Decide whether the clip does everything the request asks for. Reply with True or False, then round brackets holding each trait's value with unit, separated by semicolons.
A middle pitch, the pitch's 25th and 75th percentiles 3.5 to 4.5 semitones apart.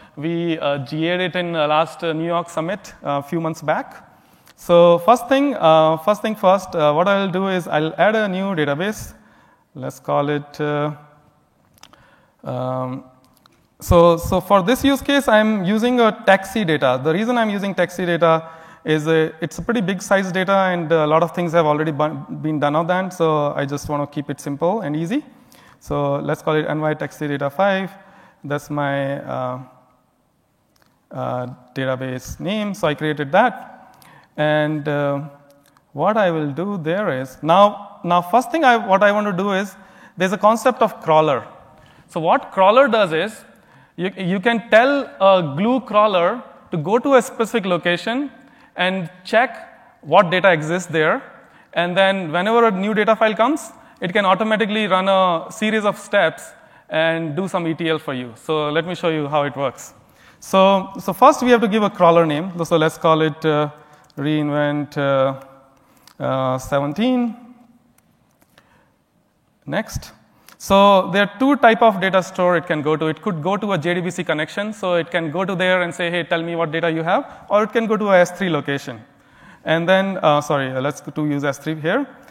False (175 Hz; 5.2 semitones)